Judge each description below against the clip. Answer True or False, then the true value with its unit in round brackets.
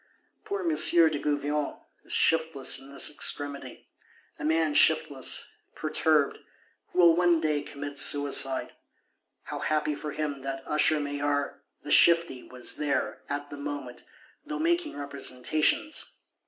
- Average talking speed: False (125 wpm)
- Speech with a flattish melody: True (2.1 semitones)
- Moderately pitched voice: True (145 Hz)